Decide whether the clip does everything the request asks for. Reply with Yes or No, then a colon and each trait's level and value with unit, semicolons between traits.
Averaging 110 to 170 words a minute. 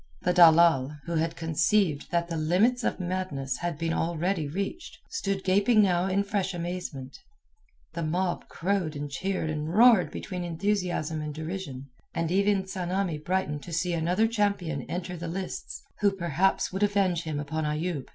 Yes: average, 160 wpm